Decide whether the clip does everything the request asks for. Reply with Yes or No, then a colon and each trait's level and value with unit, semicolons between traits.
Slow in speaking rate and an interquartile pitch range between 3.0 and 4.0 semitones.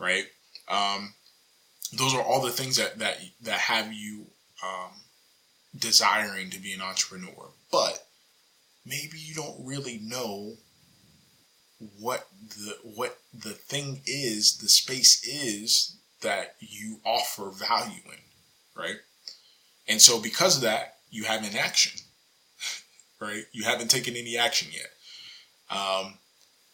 Yes: slow, 125 wpm; average, 3.5 semitones